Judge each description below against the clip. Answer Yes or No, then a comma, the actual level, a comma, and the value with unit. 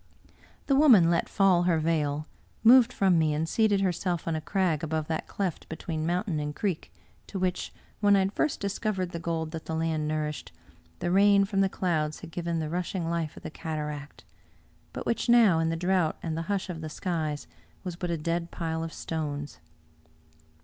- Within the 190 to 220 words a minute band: Yes, average, 195 wpm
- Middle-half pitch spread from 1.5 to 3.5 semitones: Yes, average, 3.2 semitones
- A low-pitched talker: No, medium, 170 Hz